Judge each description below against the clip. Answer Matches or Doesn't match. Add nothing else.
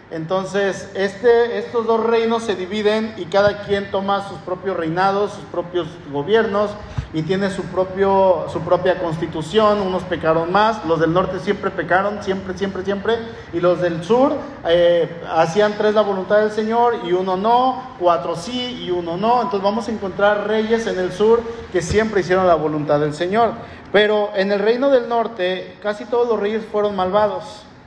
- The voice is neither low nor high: Doesn't match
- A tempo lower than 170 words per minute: Doesn't match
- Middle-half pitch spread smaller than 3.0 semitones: Doesn't match